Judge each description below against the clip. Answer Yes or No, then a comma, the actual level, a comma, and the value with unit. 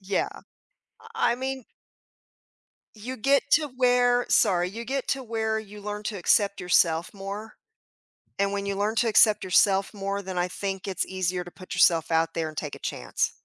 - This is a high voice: Yes, high, 200 Hz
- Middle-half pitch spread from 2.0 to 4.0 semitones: Yes, average, 3.7 semitones